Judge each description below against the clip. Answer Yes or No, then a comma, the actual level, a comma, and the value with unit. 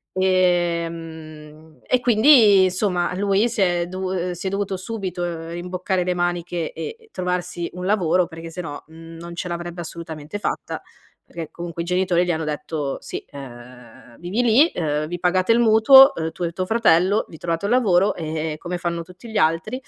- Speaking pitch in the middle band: Yes, medium, 175 Hz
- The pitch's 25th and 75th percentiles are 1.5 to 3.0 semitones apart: Yes, narrow, 2.6 semitones